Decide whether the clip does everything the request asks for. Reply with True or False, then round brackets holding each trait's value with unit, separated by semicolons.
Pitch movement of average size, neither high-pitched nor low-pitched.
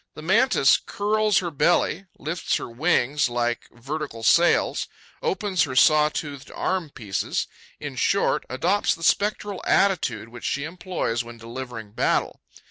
False (7.4 semitones; 150 Hz)